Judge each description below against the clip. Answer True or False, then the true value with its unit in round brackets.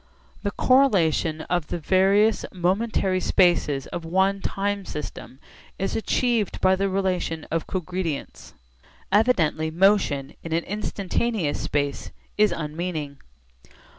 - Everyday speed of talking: False (110 wpm)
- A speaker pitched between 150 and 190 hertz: True (185 Hz)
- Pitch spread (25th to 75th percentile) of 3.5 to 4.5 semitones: True (3.9 semitones)